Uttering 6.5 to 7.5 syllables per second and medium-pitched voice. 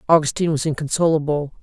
Yes: 6.9 syllables/s; medium, 155 Hz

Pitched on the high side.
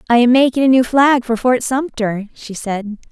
Yes: high, 245 Hz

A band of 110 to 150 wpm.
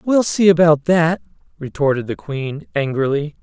Yes: average, 140 wpm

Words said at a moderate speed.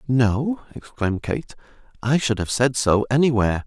Yes: average, 145 wpm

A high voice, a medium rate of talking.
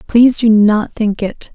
Yes: high, 220 Hz; average, 195 wpm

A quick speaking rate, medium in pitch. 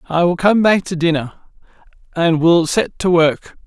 No: average, 180 wpm; medium, 170 Hz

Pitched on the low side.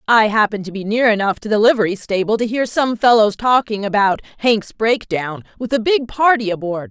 No: high, 220 Hz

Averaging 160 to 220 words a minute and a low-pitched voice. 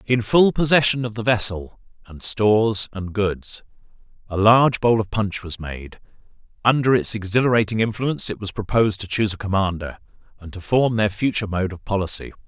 Yes: average, 175 wpm; low, 105 Hz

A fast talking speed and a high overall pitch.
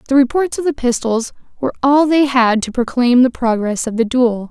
Yes: fast, 215 wpm; very high, 250 Hz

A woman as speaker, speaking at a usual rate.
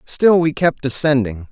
No: male; average, 160 wpm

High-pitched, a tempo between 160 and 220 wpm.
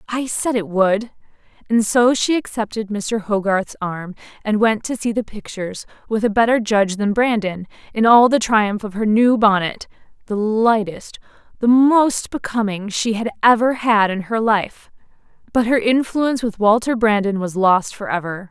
Yes: high, 215 Hz; average, 170 wpm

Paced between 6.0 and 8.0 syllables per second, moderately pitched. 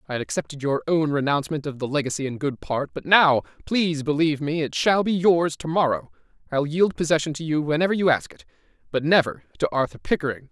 Yes: 6.2 syllables/s; medium, 145 Hz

